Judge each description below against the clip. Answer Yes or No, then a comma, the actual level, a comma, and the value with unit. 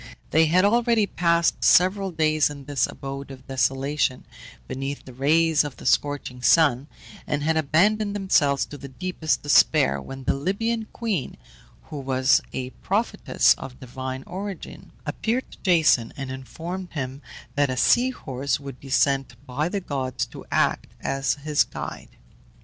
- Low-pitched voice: No, medium, 145 Hz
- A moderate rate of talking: Yes, average, 155 wpm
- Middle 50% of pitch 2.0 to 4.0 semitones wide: No, average, 5.0 semitones